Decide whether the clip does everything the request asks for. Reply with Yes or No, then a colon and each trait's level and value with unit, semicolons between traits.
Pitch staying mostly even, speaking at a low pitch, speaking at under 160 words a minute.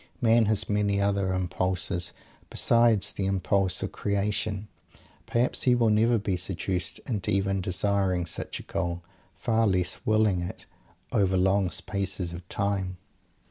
Yes: narrow, 2.3 semitones; low, 100 Hz; average, 140 wpm